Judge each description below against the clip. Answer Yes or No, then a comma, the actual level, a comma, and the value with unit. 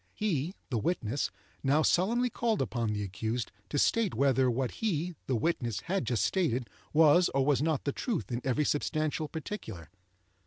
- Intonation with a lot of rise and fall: Yes, wide, 6.2 semitones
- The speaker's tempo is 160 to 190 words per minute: Yes, average, 165 wpm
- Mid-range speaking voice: Yes, medium, 145 Hz